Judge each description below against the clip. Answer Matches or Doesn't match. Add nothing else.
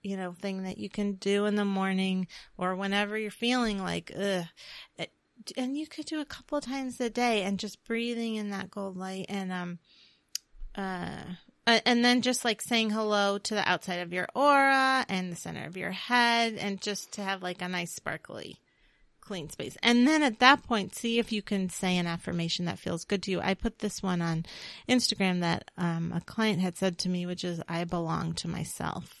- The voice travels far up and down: Doesn't match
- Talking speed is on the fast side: Matches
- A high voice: Matches